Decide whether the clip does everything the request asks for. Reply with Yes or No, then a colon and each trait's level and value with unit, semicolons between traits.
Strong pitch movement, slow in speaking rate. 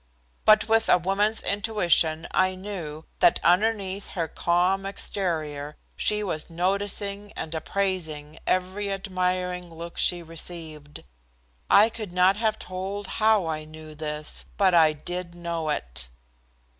No: average, 3.8 semitones; slow, 130 wpm